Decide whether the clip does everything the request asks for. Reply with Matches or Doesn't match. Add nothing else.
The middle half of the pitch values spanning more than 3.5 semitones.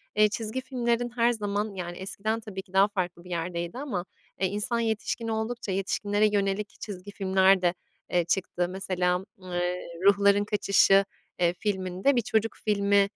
Doesn't match